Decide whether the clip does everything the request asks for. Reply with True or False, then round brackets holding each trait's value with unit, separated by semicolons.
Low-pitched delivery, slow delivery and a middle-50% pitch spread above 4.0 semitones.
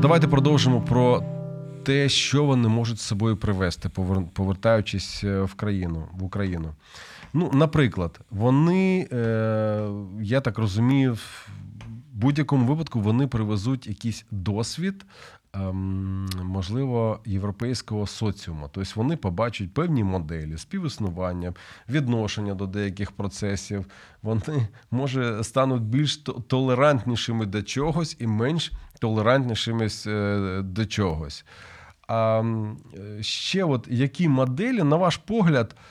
True (115 Hz; 100 wpm; 5.0 semitones)